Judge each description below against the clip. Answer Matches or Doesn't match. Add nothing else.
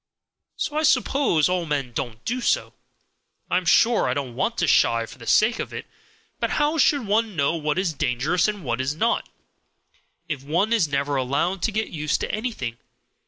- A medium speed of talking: Matches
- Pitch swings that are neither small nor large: Doesn't match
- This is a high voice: Doesn't match